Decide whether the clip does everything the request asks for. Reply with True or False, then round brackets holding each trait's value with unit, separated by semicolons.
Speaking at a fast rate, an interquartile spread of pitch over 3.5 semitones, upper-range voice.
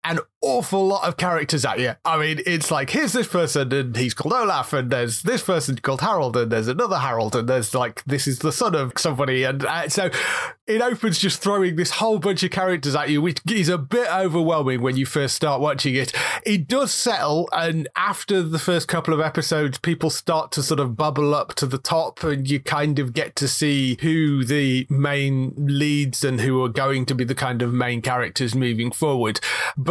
False (215 wpm; 4.3 semitones; 150 Hz)